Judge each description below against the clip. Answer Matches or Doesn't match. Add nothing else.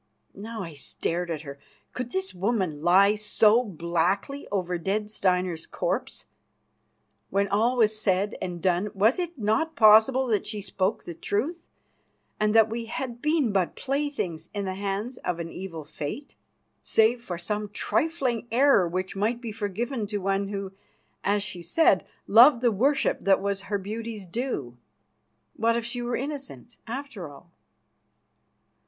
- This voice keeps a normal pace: Matches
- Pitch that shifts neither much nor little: Matches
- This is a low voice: Doesn't match